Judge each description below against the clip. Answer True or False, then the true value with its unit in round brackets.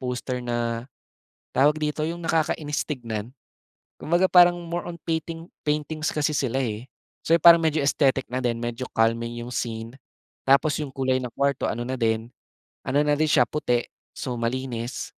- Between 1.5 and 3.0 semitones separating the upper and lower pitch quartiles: False (4.3 semitones)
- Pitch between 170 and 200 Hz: False (135 Hz)